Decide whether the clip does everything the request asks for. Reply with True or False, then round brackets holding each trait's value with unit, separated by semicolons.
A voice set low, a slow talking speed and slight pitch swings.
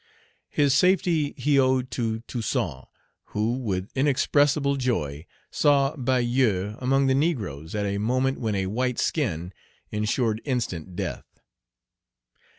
False (125 Hz; 120 wpm; 4.6 semitones)